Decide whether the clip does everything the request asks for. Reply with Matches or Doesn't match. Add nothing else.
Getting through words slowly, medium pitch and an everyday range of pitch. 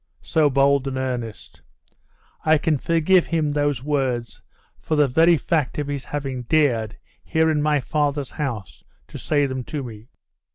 Doesn't match